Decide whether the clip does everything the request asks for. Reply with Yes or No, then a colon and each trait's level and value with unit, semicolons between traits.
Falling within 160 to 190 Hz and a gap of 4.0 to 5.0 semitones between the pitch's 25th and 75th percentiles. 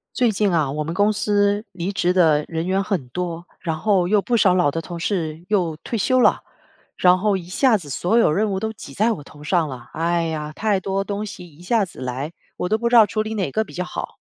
Yes: medium, 185 Hz; average, 4.3 semitones